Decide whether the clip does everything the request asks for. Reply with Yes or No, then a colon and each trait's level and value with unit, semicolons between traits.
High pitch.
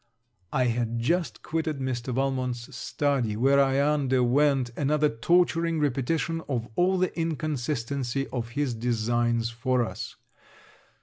No: low, 135 Hz